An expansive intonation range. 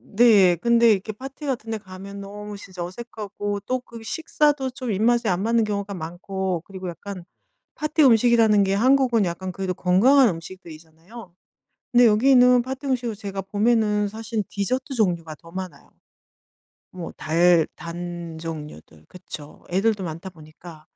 No: average, 4.9 semitones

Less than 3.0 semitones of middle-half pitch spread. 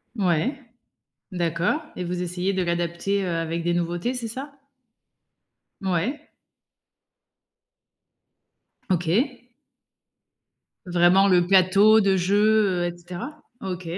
No: average, 3.3 semitones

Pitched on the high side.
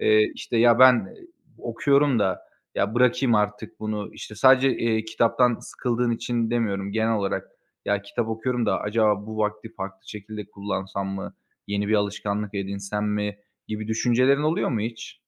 No: low, 110 Hz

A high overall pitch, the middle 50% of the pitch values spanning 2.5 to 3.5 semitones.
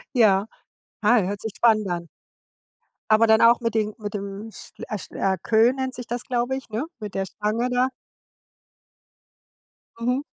Yes: high, 220 Hz; average, 2.8 semitones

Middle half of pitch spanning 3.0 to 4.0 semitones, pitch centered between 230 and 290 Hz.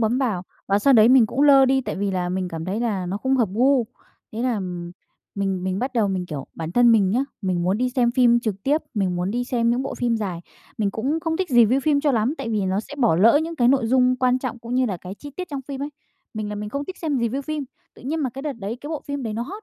No: average, 5.1 semitones; high, 235 Hz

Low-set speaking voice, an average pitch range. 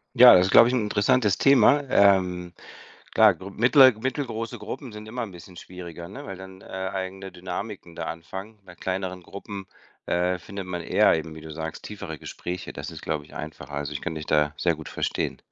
Yes: very low, 95 Hz; average, 3.5 semitones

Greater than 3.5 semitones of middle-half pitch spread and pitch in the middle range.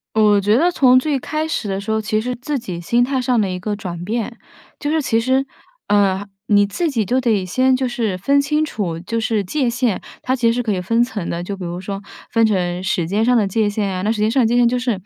No: average, 4.2 semitones; high, 225 Hz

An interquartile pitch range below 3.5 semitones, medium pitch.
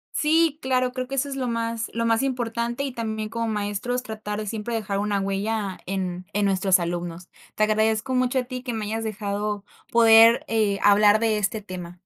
No: average, 2.7 semitones; high, 220 Hz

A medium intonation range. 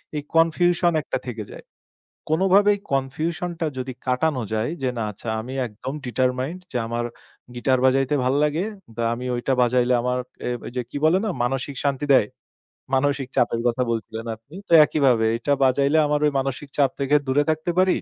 Yes: average, 3.4 semitones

